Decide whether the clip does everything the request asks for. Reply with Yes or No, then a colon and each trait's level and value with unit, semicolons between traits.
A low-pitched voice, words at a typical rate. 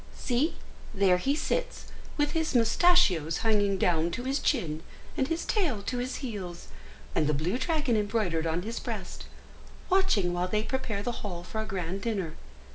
No: high, 215 Hz; average, 170 wpm